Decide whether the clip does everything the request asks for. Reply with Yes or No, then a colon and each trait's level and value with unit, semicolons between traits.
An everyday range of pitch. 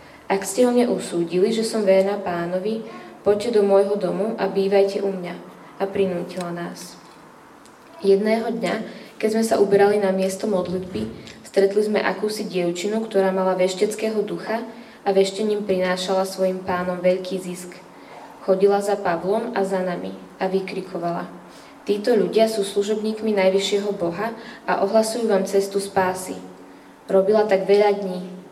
No: narrow, 2.3 semitones